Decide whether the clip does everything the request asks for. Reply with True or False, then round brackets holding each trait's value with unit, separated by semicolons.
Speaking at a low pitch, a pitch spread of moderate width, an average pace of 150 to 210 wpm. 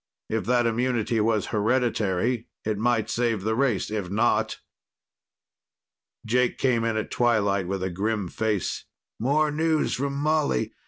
False (115 Hz; 3.0 semitones; 140 wpm)